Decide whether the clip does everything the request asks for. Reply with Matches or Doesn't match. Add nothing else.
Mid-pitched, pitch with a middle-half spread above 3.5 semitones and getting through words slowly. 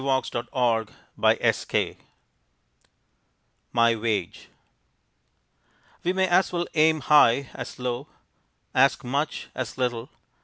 Doesn't match